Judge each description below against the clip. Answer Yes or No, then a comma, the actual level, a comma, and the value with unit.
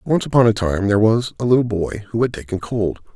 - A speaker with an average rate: No, fast, 250 wpm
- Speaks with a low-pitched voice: Yes, low, 110 Hz